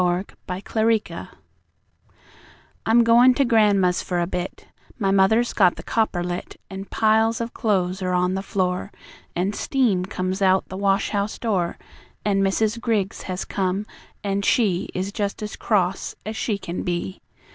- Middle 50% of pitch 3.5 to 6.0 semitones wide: No, average, 3.0 semitones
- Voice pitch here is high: Yes, high, 195 Hz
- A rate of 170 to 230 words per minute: No, average, 160 wpm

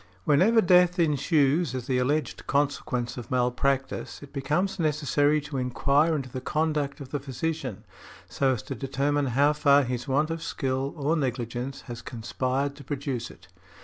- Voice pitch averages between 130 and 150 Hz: Yes, medium, 140 Hz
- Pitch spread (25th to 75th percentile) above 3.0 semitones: No, average, 2.7 semitones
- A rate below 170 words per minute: Yes, average, 160 wpm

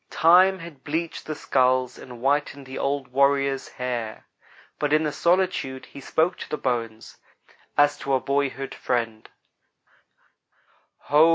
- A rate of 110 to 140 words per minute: Yes, slow, 135 wpm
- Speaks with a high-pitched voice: No, medium, 140 Hz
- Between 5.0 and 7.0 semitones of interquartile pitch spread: No, average, 3.0 semitones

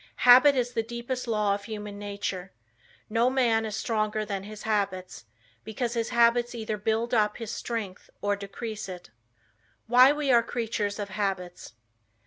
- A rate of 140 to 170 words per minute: Yes, average, 155 wpm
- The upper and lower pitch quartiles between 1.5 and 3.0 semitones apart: Yes, average, 2.7 semitones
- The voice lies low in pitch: No, high, 220 Hz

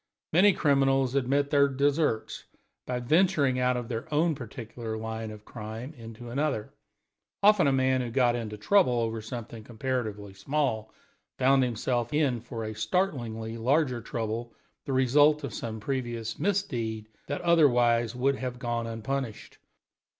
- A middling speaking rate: Yes, average, 145 wpm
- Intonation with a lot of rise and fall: No, average, 3.5 semitones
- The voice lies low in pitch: Yes, low, 125 Hz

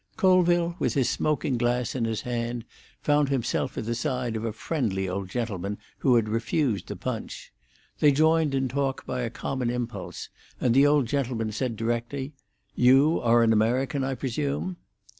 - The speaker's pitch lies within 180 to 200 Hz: No, low, 125 Hz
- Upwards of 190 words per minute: No, average, 170 wpm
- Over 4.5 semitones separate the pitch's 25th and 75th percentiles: No, average, 3.5 semitones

